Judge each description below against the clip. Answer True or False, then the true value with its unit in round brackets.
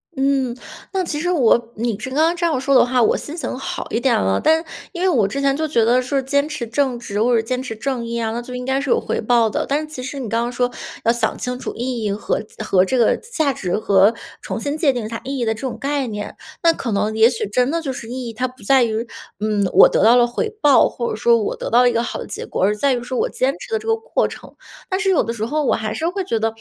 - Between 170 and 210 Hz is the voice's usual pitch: False (250 Hz)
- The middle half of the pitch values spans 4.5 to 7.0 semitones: False (3.5 semitones)